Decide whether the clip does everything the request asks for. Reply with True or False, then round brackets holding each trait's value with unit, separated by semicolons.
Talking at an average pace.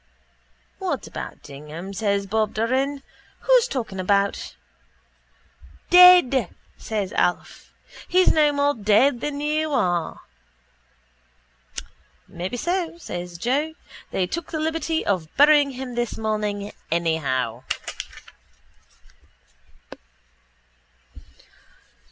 False (90 wpm)